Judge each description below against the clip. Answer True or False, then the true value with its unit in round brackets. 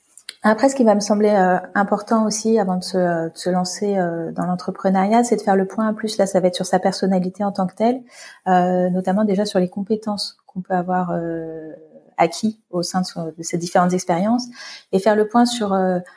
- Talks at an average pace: False (230 wpm)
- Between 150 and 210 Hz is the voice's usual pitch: True (190 Hz)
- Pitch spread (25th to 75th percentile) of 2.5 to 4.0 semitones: True (2.9 semitones)